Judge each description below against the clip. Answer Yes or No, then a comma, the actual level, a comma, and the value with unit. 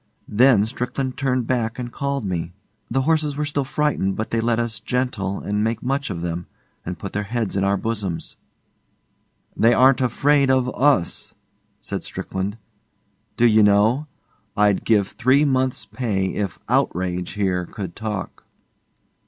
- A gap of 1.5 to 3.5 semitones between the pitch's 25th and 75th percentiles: No, average, 4.7 semitones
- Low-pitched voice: Yes, low, 115 Hz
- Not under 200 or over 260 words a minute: No, average, 150 wpm